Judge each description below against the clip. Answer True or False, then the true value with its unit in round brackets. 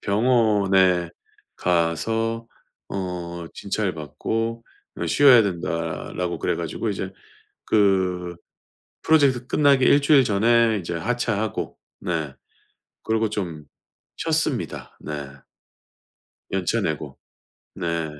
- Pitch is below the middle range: True (100 Hz)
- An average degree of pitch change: True (5.0 semitones)